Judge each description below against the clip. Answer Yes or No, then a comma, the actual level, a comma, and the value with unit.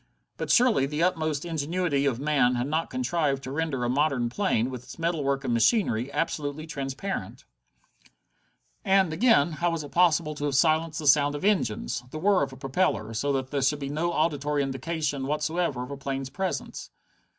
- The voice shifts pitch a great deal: No, average, 3.5 semitones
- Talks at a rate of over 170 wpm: Yes, average, 185 wpm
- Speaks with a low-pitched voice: No, medium, 145 Hz